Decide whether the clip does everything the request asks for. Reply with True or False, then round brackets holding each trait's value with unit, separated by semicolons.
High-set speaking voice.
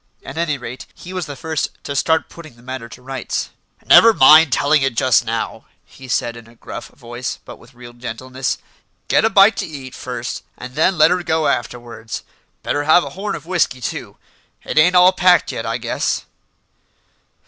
False (135 Hz)